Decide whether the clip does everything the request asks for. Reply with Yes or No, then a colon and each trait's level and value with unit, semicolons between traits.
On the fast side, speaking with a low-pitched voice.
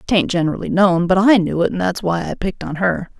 No: fast, 265 wpm; medium, 185 Hz